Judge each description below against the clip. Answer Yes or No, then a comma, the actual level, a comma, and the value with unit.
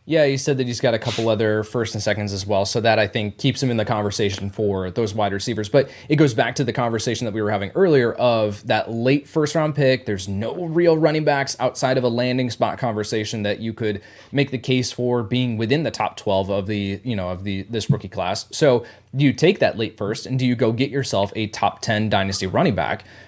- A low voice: Yes, low, 115 Hz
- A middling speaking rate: No, fast, 245 wpm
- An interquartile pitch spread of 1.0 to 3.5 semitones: No, average, 3.9 semitones